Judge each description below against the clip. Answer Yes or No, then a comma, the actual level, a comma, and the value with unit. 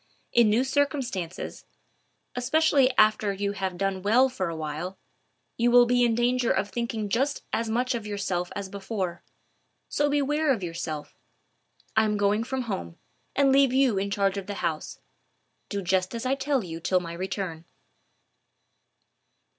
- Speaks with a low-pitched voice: No, high, 210 Hz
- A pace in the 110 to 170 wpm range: Yes, average, 160 wpm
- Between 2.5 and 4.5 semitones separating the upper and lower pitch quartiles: No, average, 5.0 semitones